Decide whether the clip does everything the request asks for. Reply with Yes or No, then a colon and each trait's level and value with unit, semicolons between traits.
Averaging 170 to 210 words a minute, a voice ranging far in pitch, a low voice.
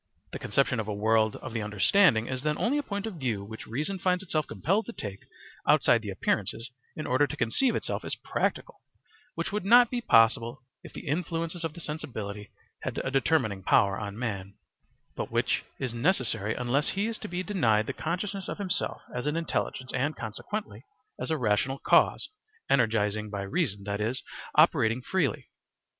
Yes: average, 180 wpm; wide, 7.6 semitones; low, 130 Hz